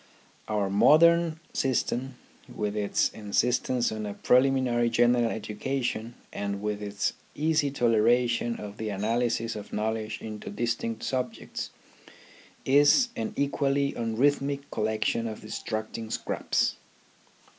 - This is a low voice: Yes, low, 115 Hz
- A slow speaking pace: Yes, slow, 115 wpm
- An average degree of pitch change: Yes, average, 3.8 semitones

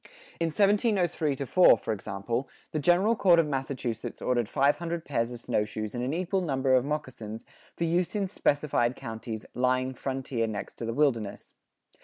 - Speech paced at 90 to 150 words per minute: No, average, 165 wpm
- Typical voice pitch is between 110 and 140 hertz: Yes, low, 135 Hz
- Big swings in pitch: Yes, wide, 6.2 semitones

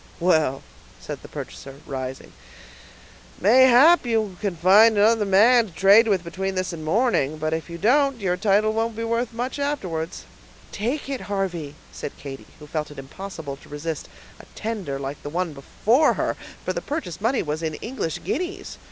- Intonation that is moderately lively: No, wide, 6.5 semitones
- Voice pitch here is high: Yes, high, 195 Hz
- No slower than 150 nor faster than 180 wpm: Yes, average, 175 wpm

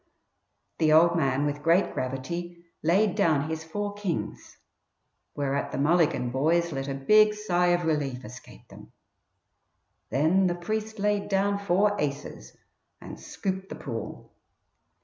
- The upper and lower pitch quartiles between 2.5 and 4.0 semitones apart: No, average, 5.3 semitones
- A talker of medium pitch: Yes, medium, 170 Hz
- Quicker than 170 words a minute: No, slow, 135 wpm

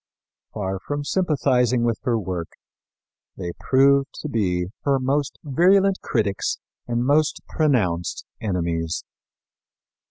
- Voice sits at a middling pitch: No, low, 125 Hz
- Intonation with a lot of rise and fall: Yes, wide, 7.2 semitones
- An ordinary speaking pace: No, slow, 105 wpm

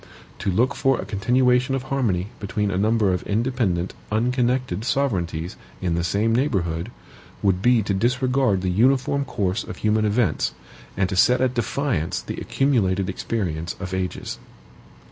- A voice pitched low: Yes, low, 110 Hz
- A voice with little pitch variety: No, average, 5.3 semitones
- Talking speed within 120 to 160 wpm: Yes, average, 150 wpm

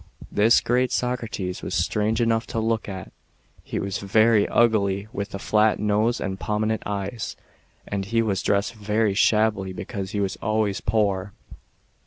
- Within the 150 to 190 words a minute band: Yes, average, 160 wpm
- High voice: No, low, 105 Hz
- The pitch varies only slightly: Yes, narrow, 2.1 semitones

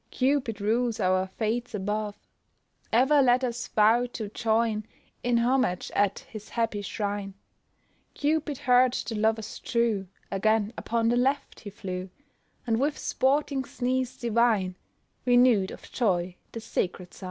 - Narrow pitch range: No, average, 3.4 semitones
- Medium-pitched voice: No, high, 225 Hz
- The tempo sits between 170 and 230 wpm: No, slow, 135 wpm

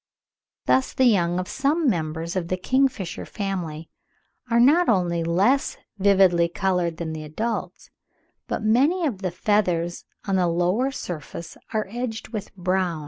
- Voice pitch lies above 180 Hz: Yes, high, 190 Hz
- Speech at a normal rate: Yes, average, 150 wpm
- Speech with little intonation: No, average, 5.3 semitones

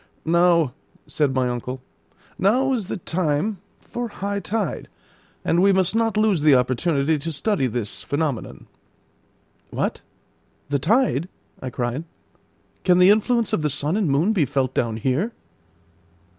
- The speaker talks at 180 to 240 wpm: No, average, 145 wpm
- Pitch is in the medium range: Yes, medium, 165 Hz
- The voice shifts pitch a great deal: Yes, wide, 6.7 semitones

